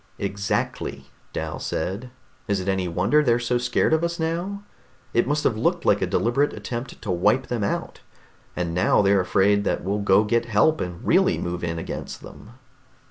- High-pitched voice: No, low, 105 Hz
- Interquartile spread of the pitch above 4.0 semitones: Yes, average, 4.6 semitones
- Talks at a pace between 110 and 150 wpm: No, average, 185 wpm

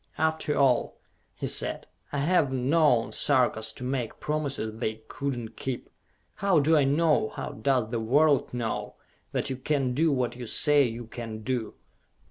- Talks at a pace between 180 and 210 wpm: No, average, 165 wpm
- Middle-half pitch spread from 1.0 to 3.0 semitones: No, average, 4.0 semitones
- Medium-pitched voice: No, low, 130 Hz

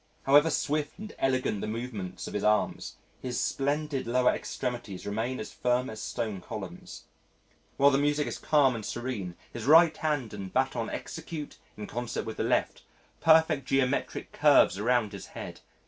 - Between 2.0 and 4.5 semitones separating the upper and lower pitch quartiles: No, average, 4.9 semitones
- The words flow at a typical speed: Yes, average, 160 wpm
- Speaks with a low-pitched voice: Yes, low, 125 Hz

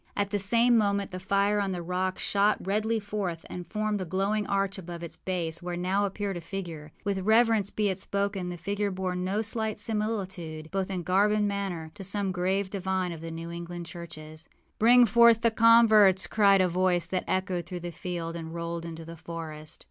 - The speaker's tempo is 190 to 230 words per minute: Yes, average, 200 wpm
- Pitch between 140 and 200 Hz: Yes, high, 190 Hz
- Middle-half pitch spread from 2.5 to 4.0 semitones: Yes, average, 2.9 semitones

